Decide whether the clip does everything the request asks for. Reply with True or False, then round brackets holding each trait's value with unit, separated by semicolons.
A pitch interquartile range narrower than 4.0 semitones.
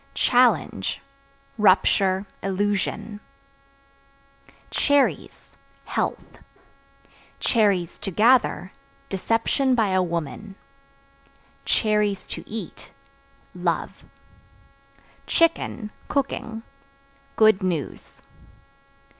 True (3.3 semitones)